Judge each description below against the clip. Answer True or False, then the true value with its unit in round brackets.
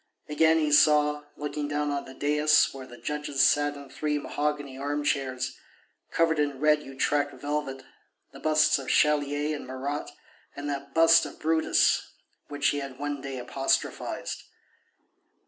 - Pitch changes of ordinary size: False (1.3 semitones)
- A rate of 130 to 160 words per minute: True (145 wpm)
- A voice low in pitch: False (145 Hz)